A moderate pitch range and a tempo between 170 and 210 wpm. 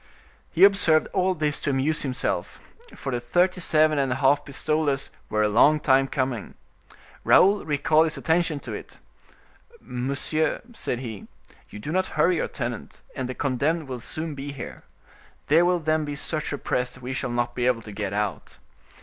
Yes: average, 3.9 semitones; average, 180 wpm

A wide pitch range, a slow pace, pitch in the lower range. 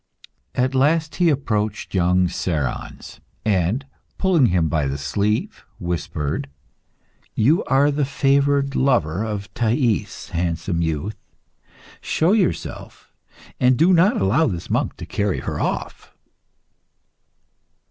Yes: wide, 8.2 semitones; slow, 115 wpm; low, 110 Hz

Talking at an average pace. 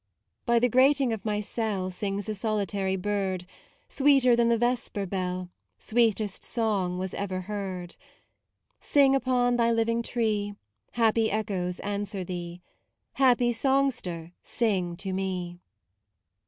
No: slow, 125 wpm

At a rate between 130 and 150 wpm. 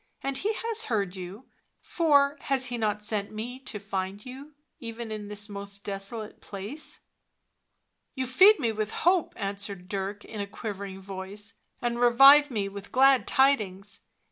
No: average, 170 wpm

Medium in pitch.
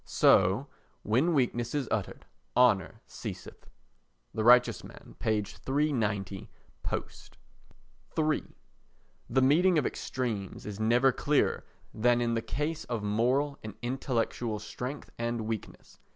No: low, 120 Hz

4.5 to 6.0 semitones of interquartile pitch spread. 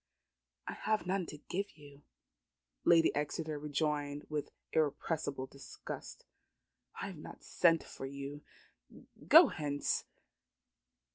No: narrow, 2.6 semitones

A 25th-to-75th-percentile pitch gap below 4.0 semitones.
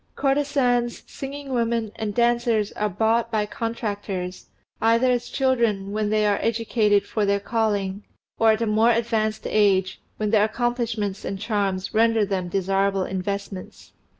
Yes: narrow, 2.6 semitones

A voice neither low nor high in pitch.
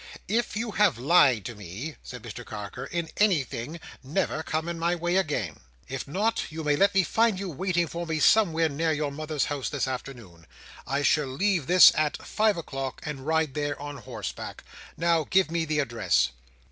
Yes: medium, 155 Hz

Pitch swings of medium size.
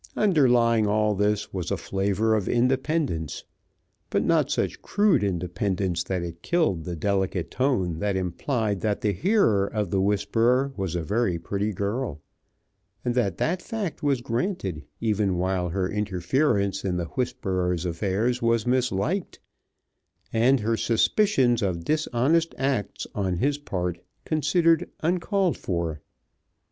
No: wide, 6.0 semitones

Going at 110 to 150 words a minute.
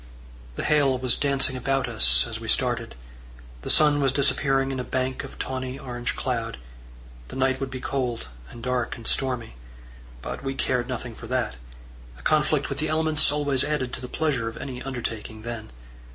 No: average, 180 wpm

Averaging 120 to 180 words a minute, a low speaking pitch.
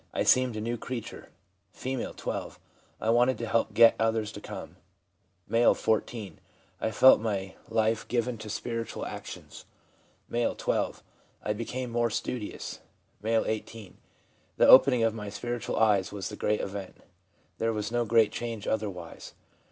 Yes: average, 160 wpm; low, 115 Hz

